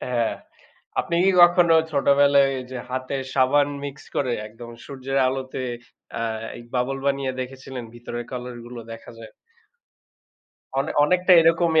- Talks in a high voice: No, low, 135 Hz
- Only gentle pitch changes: Yes, narrow, 2.3 semitones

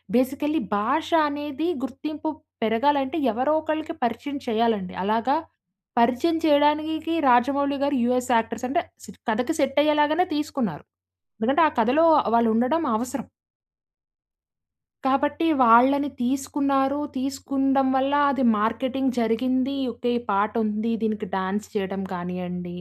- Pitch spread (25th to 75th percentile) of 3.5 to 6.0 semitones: Yes, average, 4.1 semitones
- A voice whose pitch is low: No, very high, 260 Hz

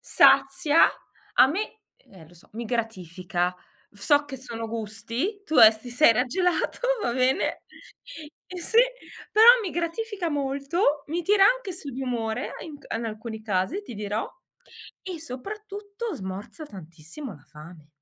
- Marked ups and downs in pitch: Yes, wide, 8.1 semitones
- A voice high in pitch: Yes, very high, 260 Hz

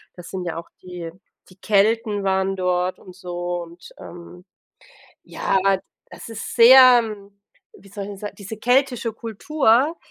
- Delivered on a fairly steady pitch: No, average, 4.3 semitones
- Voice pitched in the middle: No, high, 195 Hz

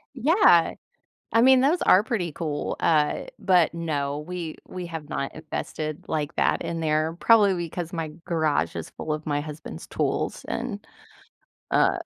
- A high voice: No, medium, 165 Hz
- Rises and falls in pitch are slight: No, average, 3.0 semitones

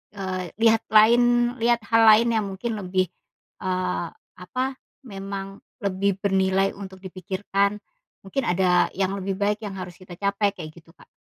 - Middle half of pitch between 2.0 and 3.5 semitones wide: Yes, narrow, 2.4 semitones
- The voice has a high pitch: Yes, high, 195 Hz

